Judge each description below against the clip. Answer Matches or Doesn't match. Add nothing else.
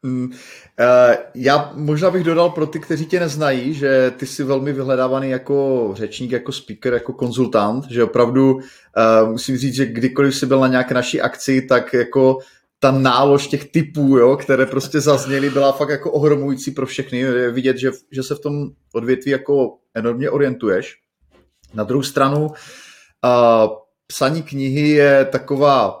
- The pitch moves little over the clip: Matches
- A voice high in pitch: Doesn't match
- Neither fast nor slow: Matches